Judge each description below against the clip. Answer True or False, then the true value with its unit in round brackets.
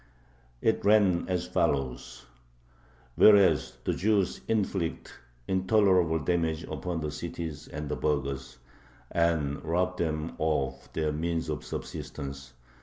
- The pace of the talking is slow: True (110 wpm)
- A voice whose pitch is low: True (80 Hz)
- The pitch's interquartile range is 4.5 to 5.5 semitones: False (3.6 semitones)